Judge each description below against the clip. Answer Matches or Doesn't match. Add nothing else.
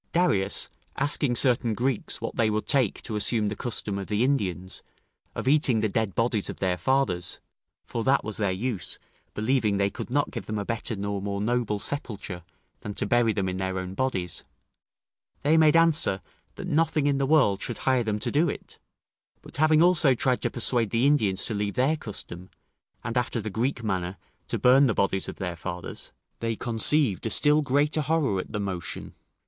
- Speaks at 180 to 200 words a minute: Matches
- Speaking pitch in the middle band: Doesn't match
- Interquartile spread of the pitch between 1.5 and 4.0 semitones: Doesn't match